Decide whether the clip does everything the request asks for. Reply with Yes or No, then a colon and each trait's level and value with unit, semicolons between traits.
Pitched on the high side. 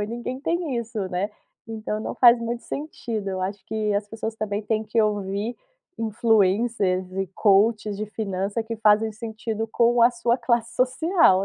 Yes: high, 220 Hz